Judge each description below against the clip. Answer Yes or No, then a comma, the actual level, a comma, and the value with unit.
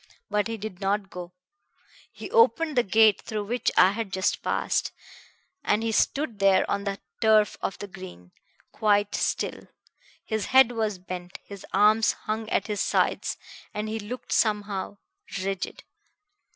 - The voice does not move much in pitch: Yes, narrow, 2.1 semitones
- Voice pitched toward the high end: Yes, high, 210 Hz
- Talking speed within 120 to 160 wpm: Yes, average, 150 wpm